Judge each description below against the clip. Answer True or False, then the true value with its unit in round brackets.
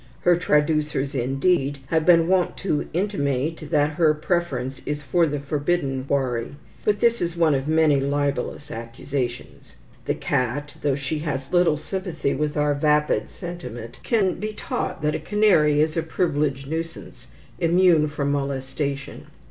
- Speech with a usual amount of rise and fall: True (3.4 semitones)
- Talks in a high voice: False (150 Hz)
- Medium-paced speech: True (150 wpm)